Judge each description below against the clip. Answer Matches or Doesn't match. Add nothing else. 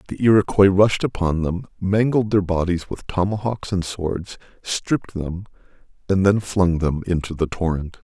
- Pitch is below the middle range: Matches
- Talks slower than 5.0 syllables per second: Matches